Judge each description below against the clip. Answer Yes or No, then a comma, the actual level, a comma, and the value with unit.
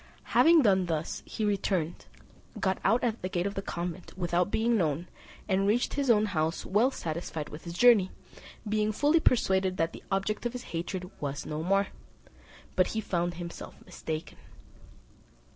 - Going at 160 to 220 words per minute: Yes, average, 165 wpm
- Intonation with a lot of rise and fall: No, average, 3.9 semitones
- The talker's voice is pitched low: No, high, 190 Hz